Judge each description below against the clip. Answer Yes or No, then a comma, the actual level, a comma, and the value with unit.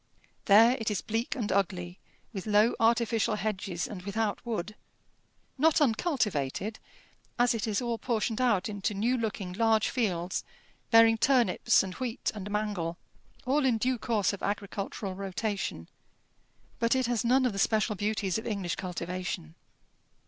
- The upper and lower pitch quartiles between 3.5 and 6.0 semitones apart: No, average, 3.1 semitones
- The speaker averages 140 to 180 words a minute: Yes, average, 150 wpm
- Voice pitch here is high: Yes, high, 215 Hz